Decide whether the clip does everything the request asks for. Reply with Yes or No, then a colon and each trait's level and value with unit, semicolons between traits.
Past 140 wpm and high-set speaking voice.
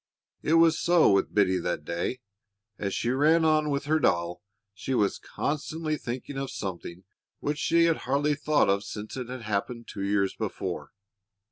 No: average, 170 wpm; low, 130 Hz